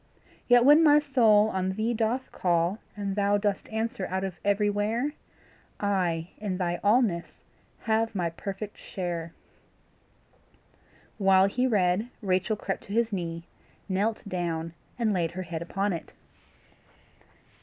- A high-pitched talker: Yes, high, 200 Hz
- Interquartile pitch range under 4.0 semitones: Yes, average, 3.4 semitones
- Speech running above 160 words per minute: No, slow, 135 wpm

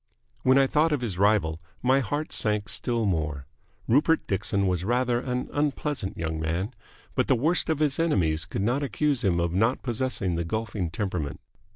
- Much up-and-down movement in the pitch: Yes, wide, 6.8 semitones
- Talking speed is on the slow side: No, average, 180 wpm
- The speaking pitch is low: Yes, low, 110 Hz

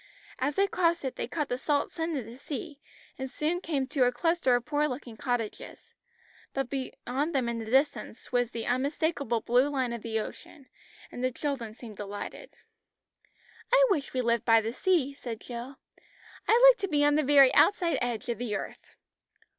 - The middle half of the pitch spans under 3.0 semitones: No, average, 3.9 semitones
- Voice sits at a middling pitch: No, very high, 265 Hz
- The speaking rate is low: No, average, 190 wpm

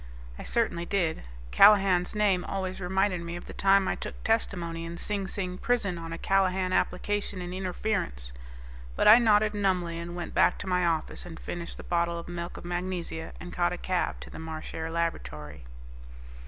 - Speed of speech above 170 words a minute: Yes, average, 180 wpm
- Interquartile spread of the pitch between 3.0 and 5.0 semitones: No, narrow, 2.4 semitones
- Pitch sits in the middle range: Yes, medium, 180 Hz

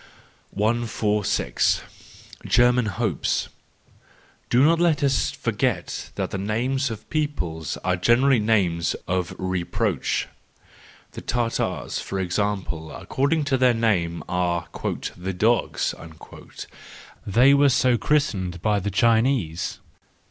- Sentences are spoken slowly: Yes, slow, 115 wpm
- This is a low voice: Yes, low, 110 Hz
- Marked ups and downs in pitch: Yes, wide, 5.9 semitones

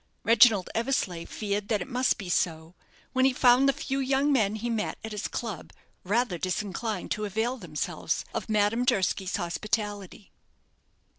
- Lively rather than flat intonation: No, average, 4.1 semitones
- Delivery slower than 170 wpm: Yes, average, 155 wpm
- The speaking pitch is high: Yes, high, 215 Hz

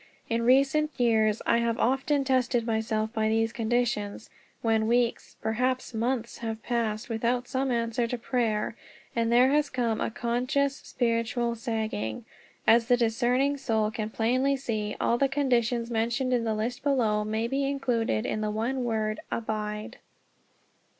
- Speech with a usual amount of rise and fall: No, narrow, 2.3 semitones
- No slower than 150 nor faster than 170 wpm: Yes, average, 155 wpm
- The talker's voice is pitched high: Yes, high, 235 Hz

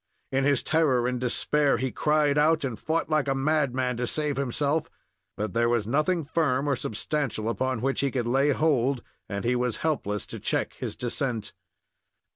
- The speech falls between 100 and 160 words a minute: No, average, 180 wpm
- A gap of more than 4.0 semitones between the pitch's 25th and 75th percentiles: No, average, 3.5 semitones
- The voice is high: No, low, 135 Hz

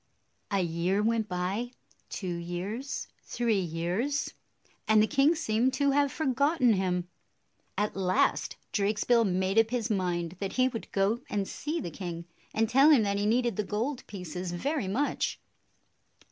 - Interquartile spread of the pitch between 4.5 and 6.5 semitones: Yes, average, 5.1 semitones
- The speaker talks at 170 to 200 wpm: No, average, 160 wpm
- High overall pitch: Yes, high, 210 Hz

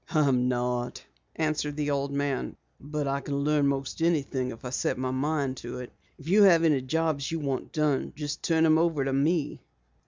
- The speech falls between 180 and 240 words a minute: Yes, average, 195 wpm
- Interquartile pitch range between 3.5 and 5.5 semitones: No, average, 2.8 semitones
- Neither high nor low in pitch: Yes, medium, 145 Hz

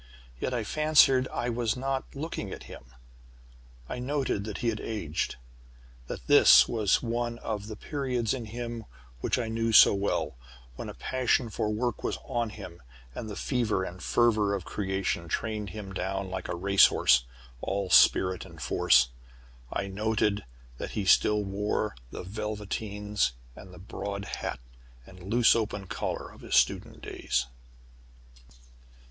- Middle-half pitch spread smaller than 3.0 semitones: No, average, 3.4 semitones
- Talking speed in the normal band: Yes, average, 155 wpm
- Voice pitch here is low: Yes, low, 105 Hz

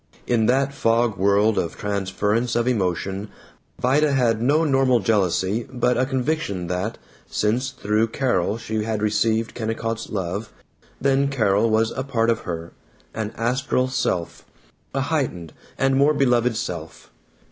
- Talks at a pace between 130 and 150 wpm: Yes, average, 140 wpm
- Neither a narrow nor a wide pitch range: Yes, average, 3.9 semitones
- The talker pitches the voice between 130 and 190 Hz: No, low, 115 Hz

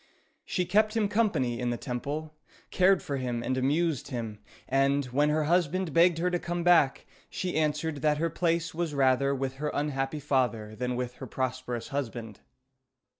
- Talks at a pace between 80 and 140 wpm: No, average, 175 wpm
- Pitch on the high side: No, medium, 145 Hz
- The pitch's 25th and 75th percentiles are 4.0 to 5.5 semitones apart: Yes, average, 4.7 semitones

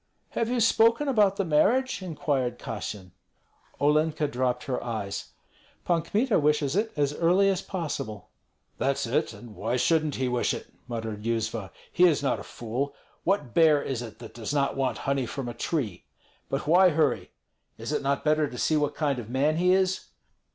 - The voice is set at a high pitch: No, medium, 145 Hz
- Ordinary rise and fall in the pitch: No, wide, 6.1 semitones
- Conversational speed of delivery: Yes, average, 180 wpm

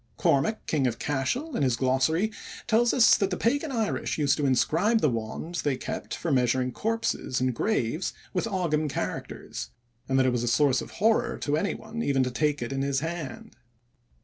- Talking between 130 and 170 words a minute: No, average, 190 wpm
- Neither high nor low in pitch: Yes, medium, 150 Hz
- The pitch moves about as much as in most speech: No, wide, 8.8 semitones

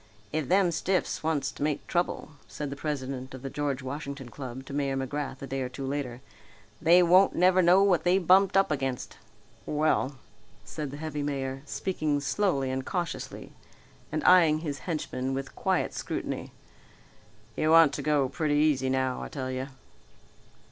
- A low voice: No, medium, 145 Hz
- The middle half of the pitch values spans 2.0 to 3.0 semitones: No, average, 3.4 semitones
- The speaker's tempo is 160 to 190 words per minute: Yes, average, 170 wpm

